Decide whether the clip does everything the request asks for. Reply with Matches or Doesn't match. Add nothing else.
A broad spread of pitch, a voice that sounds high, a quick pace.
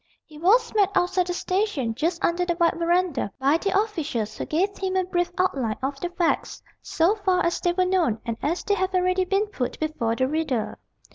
Doesn't match